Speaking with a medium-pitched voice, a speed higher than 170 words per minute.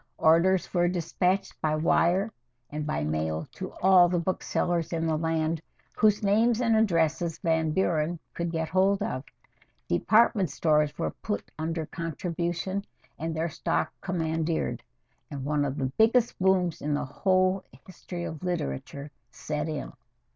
No: medium, 170 Hz; average, 145 wpm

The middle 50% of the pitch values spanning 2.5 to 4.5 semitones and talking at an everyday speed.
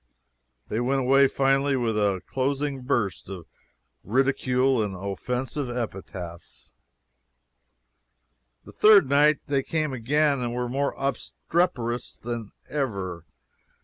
No: average, 3.9 semitones; slow, 110 wpm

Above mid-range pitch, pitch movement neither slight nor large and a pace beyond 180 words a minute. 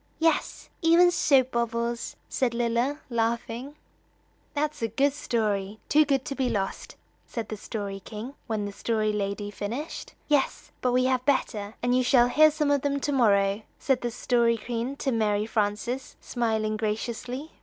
No: high, 235 Hz; average, 3.9 semitones; average, 165 wpm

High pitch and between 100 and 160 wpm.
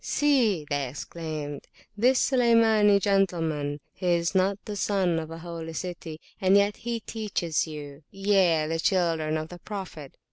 No: medium, 175 Hz; average, 145 wpm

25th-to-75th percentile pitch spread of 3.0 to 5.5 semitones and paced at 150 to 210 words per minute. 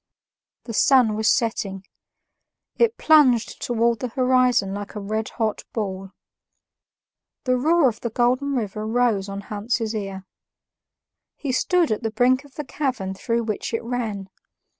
No: average, 3.4 semitones; average, 140 wpm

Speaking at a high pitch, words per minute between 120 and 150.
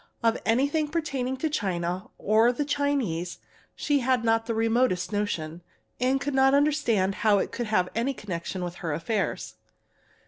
No: high, 225 Hz; average, 160 wpm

